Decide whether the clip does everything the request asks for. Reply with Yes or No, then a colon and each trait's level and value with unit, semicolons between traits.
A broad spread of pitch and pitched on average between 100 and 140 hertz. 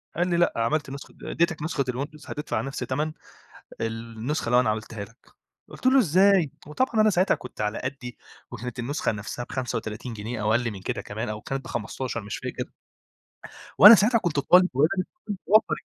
Yes: wide, 7.2 semitones; low, 135 Hz